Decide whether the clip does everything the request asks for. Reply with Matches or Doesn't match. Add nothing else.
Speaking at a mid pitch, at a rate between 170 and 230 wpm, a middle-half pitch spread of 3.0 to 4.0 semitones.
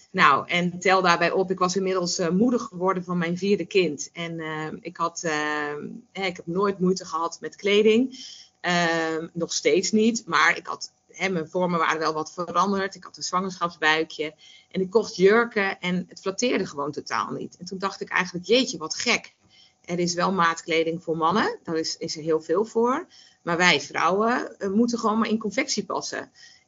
Matches